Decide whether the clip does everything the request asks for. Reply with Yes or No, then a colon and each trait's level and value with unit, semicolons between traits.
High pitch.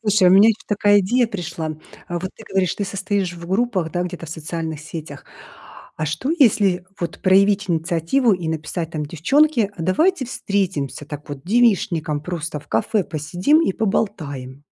No: medium, 180 Hz